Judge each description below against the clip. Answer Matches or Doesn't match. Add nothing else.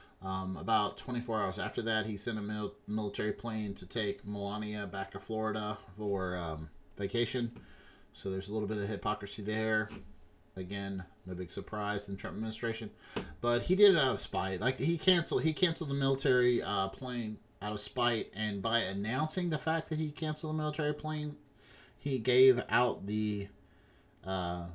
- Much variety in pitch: Doesn't match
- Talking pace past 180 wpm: Doesn't match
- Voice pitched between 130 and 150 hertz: Doesn't match